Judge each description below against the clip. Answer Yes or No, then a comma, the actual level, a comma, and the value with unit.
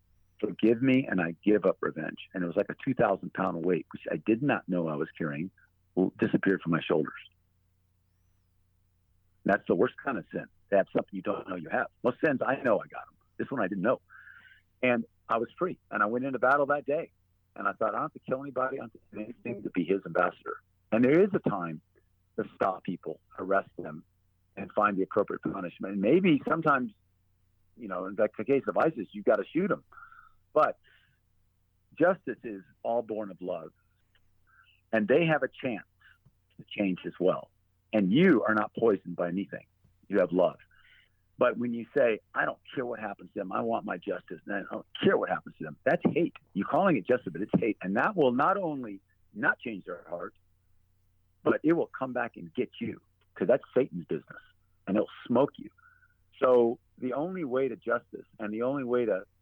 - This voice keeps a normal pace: No, fast, 210 wpm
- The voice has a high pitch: No, very low, 95 Hz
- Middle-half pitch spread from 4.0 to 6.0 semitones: Yes, average, 4.7 semitones